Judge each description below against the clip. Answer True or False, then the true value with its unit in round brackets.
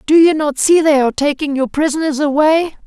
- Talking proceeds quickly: True (210 wpm)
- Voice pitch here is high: True (300 Hz)